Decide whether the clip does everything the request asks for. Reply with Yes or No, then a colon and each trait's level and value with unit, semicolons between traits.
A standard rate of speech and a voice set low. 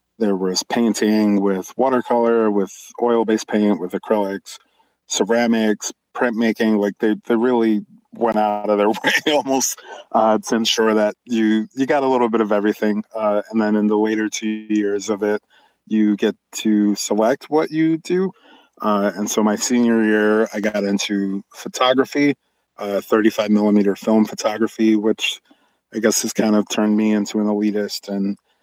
Yes: average, 165 wpm; low, 110 Hz